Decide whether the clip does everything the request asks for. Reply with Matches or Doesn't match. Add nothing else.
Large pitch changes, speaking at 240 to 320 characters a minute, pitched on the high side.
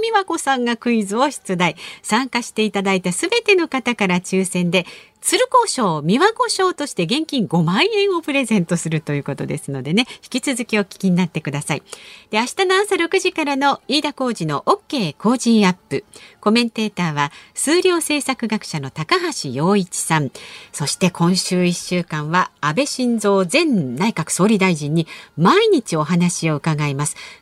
Doesn't match